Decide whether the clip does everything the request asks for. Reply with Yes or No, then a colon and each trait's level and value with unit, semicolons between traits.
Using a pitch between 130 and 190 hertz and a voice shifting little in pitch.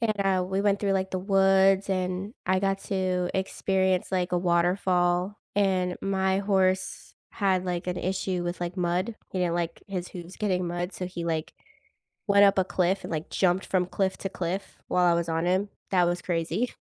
Yes: medium, 185 Hz; narrow, 1.6 semitones